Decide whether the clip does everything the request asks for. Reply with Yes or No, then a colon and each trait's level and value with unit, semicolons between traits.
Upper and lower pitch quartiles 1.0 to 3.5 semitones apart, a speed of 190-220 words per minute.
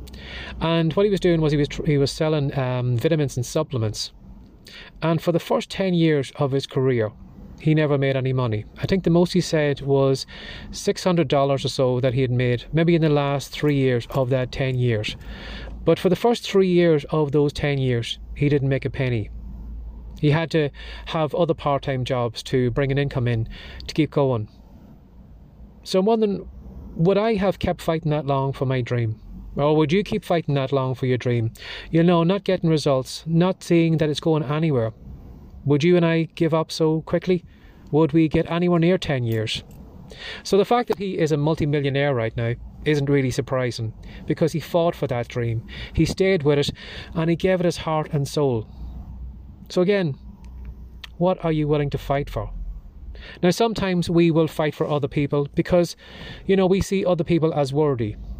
No: wide, 5.4 semitones; average, 195 wpm